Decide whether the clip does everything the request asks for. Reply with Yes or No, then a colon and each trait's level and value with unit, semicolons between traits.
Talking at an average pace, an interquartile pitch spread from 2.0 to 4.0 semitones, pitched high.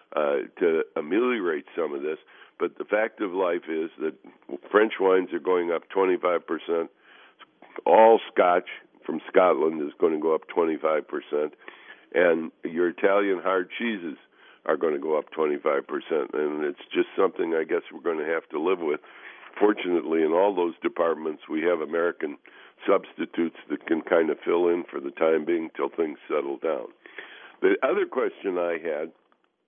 Yes: average, 170 wpm; average, 3.7 semitones; very high, 390 Hz